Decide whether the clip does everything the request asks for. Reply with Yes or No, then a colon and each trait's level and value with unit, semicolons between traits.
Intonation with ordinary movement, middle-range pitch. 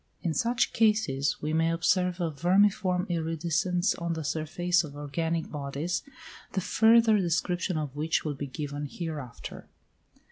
Yes: average, 3.2 semitones; medium, 165 Hz